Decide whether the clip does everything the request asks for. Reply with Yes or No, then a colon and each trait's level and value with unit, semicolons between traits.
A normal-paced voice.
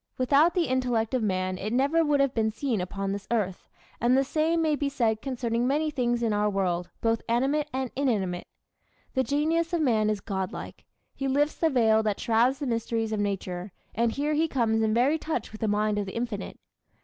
No: fast, 210 wpm